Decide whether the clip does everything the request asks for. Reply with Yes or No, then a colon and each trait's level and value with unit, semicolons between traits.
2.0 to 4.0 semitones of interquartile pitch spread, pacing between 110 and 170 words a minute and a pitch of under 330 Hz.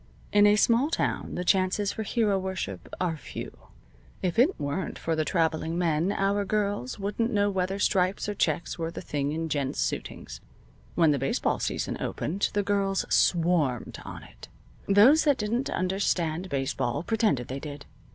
No: average, 4.5 semitones; average, 165 wpm; medium, 185 Hz